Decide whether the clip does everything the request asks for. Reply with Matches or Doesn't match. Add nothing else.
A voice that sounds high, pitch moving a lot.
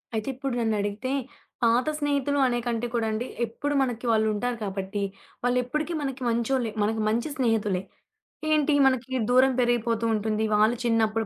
Doesn't match